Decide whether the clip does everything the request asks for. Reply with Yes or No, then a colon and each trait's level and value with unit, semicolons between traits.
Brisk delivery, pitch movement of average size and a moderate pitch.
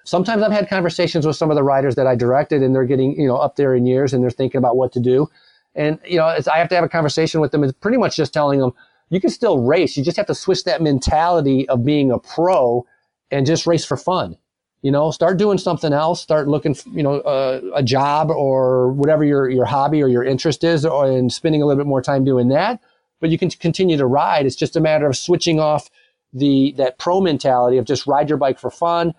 Yes: fast, 255 wpm; average, 3.7 semitones; medium, 145 Hz